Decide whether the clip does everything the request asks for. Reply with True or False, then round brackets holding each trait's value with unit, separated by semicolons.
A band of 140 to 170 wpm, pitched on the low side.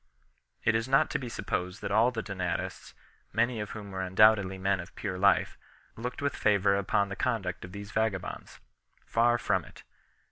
False (180 wpm; 100 Hz)